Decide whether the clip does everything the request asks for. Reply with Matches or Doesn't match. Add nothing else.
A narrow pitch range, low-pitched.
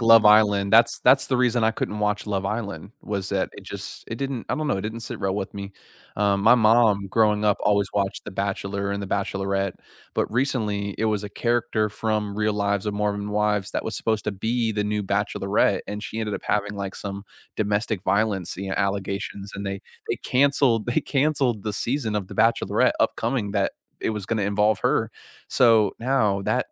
Matches